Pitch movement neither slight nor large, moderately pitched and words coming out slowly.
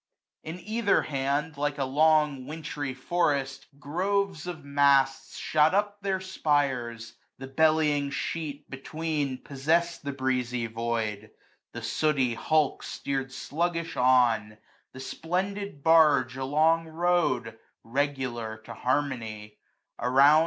Yes: average, 3.7 semitones; medium, 145 Hz; slow, 115 wpm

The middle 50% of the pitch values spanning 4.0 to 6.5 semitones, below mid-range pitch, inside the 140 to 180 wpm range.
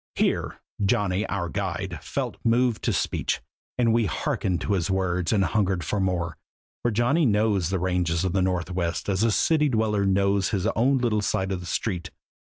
No: average, 3.4 semitones; low, 100 Hz; average, 170 wpm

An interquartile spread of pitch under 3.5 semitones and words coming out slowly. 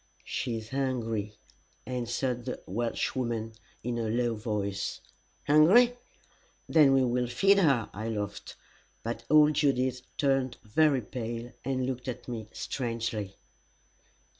Yes: average, 2.9 semitones; slow, 120 wpm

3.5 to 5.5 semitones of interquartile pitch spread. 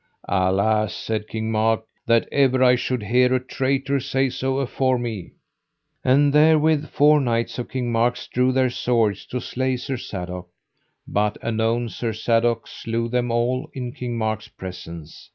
No: average, 2.8 semitones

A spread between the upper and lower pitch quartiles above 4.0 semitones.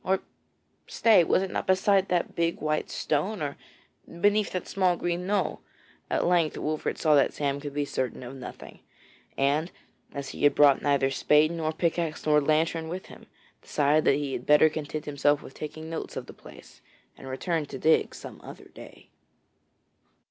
No: average, 3.1 semitones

